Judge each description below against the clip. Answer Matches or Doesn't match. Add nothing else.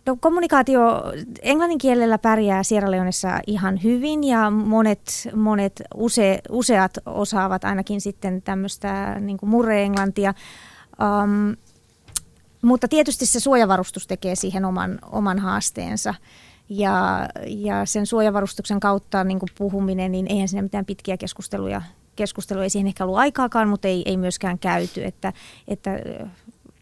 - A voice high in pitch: Matches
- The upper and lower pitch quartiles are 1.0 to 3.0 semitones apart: Matches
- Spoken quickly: Doesn't match